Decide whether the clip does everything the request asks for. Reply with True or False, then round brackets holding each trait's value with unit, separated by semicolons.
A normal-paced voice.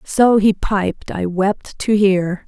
True (170 wpm)